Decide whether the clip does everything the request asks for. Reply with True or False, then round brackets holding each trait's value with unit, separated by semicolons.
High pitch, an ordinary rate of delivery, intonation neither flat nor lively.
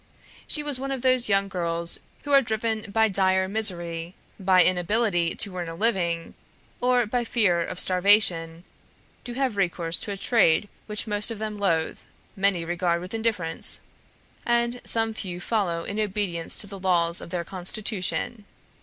True (195 Hz; 165 wpm; 4.2 semitones)